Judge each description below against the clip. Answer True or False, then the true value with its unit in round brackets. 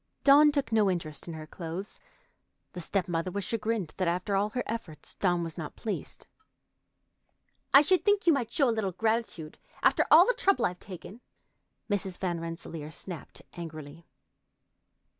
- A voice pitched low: False (190 Hz)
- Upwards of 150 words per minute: True (160 wpm)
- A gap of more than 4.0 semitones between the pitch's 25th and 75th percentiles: True (5.4 semitones)